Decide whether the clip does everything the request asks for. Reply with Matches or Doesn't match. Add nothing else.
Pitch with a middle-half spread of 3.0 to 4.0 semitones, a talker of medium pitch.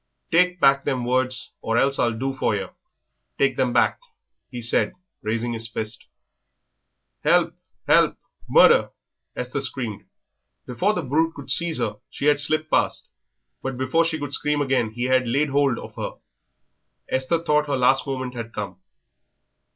Doesn't match